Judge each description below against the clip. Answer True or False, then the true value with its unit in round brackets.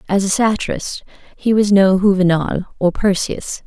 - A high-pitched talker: True (195 Hz)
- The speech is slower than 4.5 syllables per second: False (4.9 syllables/s)